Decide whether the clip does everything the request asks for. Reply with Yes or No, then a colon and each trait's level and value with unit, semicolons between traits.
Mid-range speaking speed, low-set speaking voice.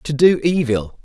No: average, 175 wpm; medium, 145 Hz